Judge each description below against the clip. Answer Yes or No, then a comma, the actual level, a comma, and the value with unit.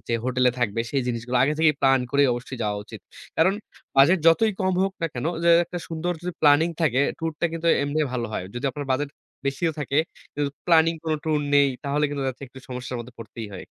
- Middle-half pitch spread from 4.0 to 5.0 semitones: Yes, average, 4.3 semitones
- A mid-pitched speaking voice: Yes, medium, 145 Hz